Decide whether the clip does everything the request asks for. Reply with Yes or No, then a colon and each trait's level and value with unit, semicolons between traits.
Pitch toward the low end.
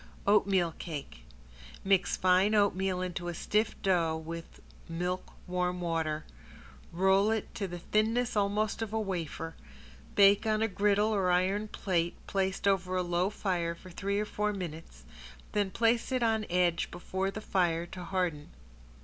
No: high, 190 Hz